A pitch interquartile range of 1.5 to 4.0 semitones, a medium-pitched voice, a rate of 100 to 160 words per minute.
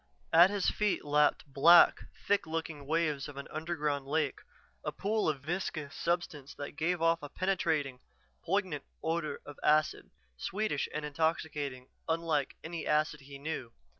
Yes: average, 2.7 semitones; medium, 155 Hz; average, 145 wpm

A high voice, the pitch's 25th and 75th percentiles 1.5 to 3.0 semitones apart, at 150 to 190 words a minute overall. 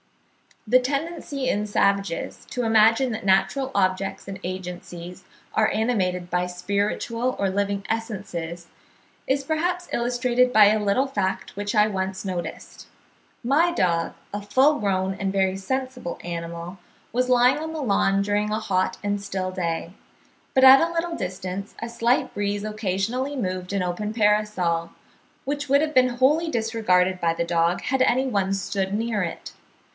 No: high, 205 Hz; average, 5.1 semitones; average, 155 wpm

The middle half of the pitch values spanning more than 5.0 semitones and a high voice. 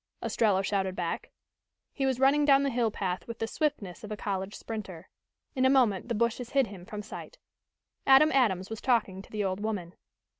Yes: wide, 5.4 semitones; high, 220 Hz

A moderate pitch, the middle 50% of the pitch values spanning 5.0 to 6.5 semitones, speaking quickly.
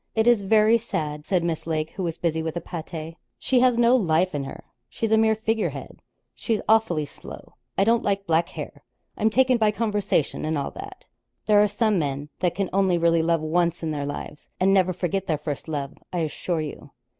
Yes: medium, 180 Hz; average, 5.3 semitones; fast, 210 wpm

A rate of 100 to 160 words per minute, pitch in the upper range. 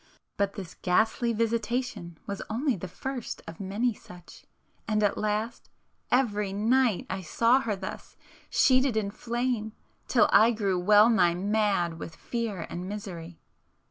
Yes: average, 140 wpm; high, 210 Hz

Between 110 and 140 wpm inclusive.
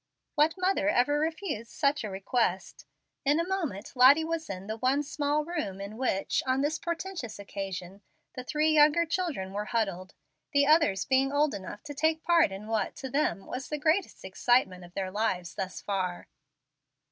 No: average, 175 wpm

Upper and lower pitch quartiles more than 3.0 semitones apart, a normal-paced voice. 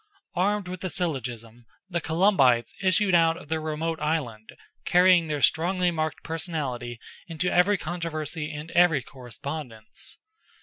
No: average, 4.2 semitones; slow, 130 wpm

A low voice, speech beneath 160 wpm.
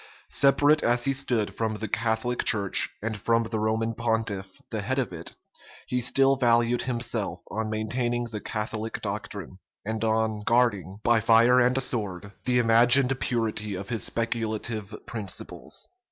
Yes: low, 115 Hz; average, 150 wpm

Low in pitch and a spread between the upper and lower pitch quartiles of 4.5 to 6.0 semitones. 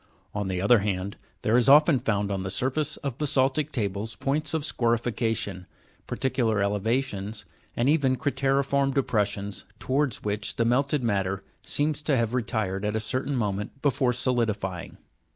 Yes: low, 120 Hz; average, 4.9 semitones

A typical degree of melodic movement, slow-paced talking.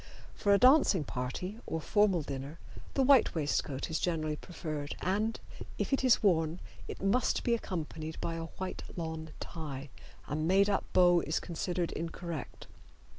No: average, 4.1 semitones; average, 155 wpm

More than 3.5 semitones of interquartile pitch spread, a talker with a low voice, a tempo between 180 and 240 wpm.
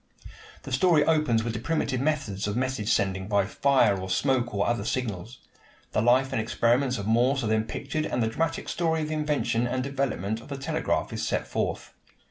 Yes: average, 4.1 semitones; low, 125 Hz; average, 200 wpm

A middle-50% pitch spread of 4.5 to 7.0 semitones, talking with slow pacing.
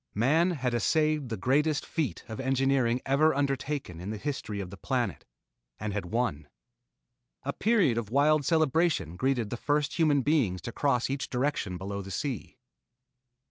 No: average, 5.2 semitones; average, 160 wpm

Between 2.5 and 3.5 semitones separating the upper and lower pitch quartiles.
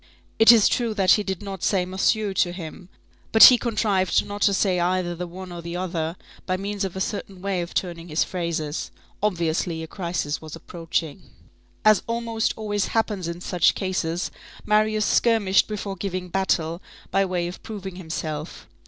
Yes: average, 3.1 semitones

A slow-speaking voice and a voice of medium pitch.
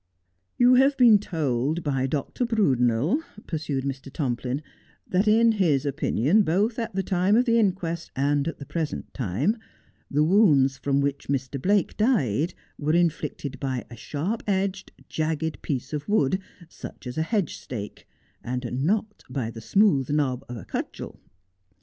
No: average, 165 wpm; medium, 150 Hz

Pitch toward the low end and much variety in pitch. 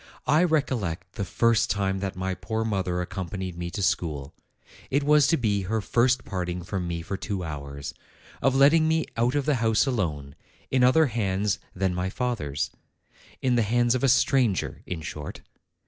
Yes: low, 100 Hz; wide, 5.9 semitones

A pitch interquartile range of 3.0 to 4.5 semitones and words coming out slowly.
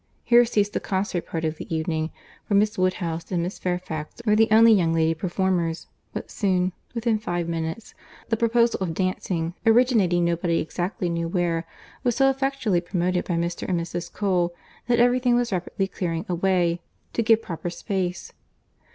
No: average, 4.2 semitones; average, 165 wpm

